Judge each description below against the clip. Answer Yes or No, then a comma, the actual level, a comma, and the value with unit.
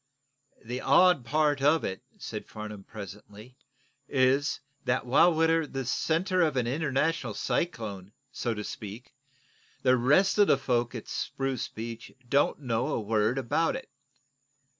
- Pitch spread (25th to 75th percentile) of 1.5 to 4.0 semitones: No, average, 5.2 semitones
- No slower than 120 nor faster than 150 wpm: Yes, average, 140 wpm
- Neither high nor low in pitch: No, low, 130 Hz